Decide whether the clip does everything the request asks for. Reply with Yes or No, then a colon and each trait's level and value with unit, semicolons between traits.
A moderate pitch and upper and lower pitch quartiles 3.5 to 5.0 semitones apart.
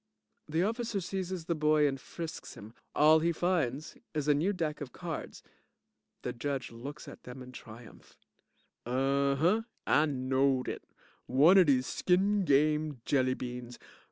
Yes: medium, 150 Hz; average, 4.6 semitones